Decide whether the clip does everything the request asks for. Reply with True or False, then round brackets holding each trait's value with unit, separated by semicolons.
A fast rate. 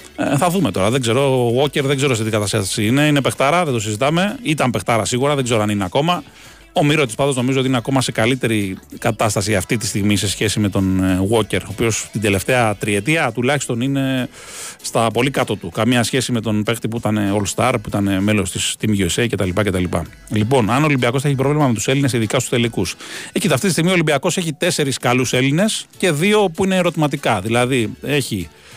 True (210 wpm)